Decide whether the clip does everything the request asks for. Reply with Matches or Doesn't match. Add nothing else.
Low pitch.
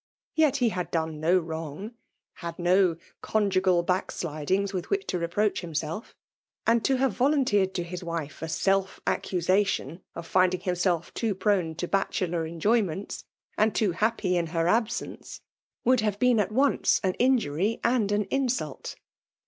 Doesn't match